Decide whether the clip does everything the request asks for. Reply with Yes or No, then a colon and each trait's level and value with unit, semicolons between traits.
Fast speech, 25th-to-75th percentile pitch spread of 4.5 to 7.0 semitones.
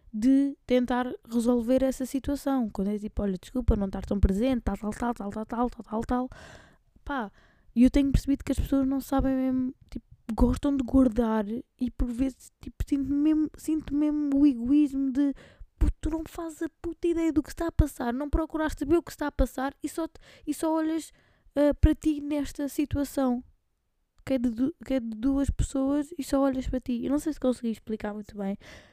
No: fast, 210 wpm; average, 3.0 semitones